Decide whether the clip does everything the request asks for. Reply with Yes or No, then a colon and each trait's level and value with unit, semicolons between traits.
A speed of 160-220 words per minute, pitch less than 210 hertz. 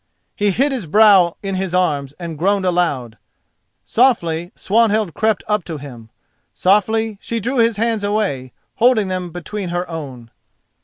No: average, 145 wpm; high, 190 Hz